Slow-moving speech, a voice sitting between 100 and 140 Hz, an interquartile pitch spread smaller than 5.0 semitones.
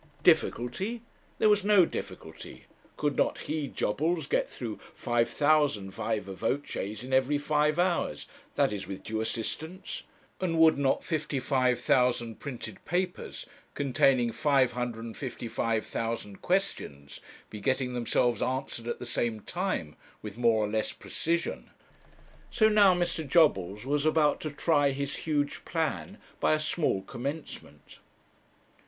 No: slow, 125 wpm; low, 135 Hz; wide, 5.5 semitones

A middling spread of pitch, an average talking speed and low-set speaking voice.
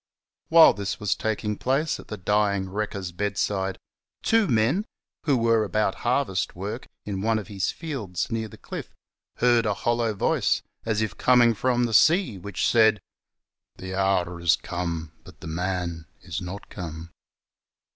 Yes: average, 3.9 semitones; average, 160 wpm; low, 105 Hz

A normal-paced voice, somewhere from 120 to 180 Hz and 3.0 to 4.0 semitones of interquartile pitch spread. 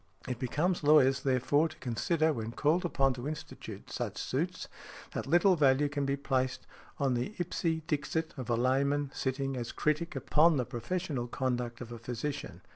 Yes: average, 170 wpm; medium, 140 Hz; average, 3.6 semitones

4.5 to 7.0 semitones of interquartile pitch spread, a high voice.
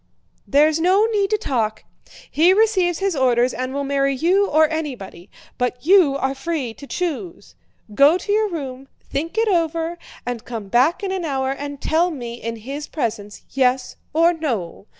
Yes: wide, 5.4 semitones; very high, 290 Hz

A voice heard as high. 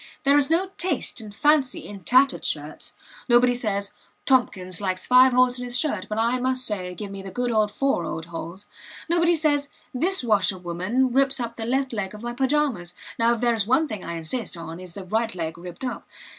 Yes: high, 235 Hz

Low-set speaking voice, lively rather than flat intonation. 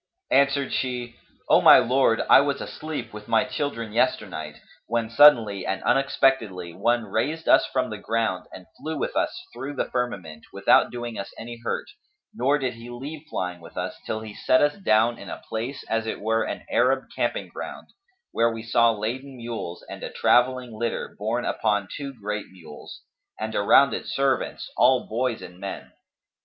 No: low, 115 Hz; average, 3.7 semitones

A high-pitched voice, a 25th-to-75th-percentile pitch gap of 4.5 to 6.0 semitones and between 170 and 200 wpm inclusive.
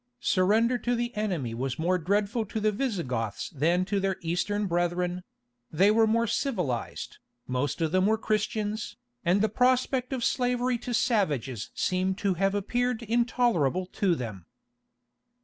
No: high, 200 Hz; average, 5.0 semitones; average, 150 wpm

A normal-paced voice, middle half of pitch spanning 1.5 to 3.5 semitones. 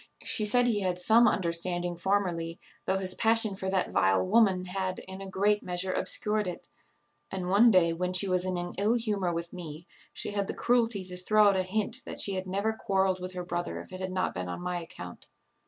No: fast, 220 wpm; narrow, 2.5 semitones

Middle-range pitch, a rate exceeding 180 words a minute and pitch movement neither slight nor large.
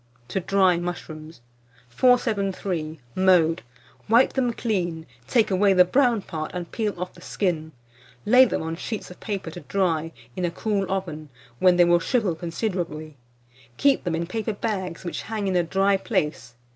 No: medium, 180 Hz; average, 165 wpm; average, 3.7 semitones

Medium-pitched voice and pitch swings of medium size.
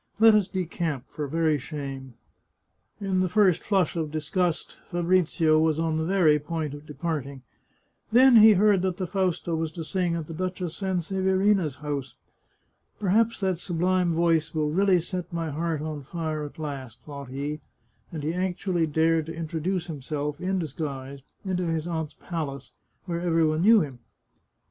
Yes: medium, 165 Hz; average, 3.4 semitones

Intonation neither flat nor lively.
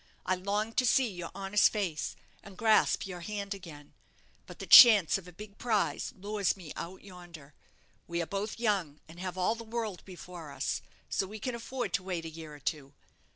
Yes: average, 3.8 semitones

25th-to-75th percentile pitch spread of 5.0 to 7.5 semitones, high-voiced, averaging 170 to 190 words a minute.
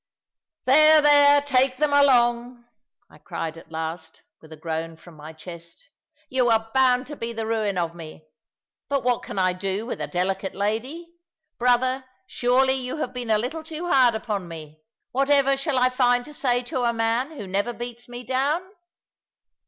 Yes: wide, 5.6 semitones; high, 245 Hz; average, 175 wpm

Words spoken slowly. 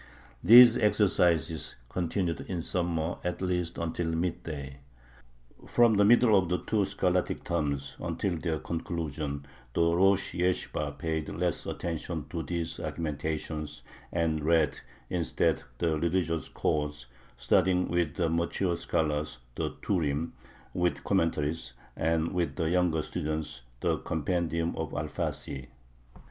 Yes: slow, 120 wpm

